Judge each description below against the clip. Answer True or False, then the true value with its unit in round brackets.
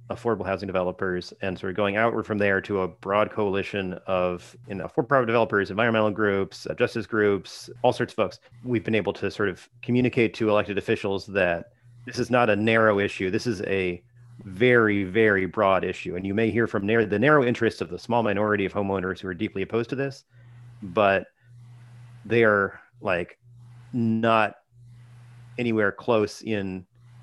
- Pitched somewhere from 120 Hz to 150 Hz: False (110 Hz)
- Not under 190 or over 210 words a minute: False (175 wpm)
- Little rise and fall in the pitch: False (3.4 semitones)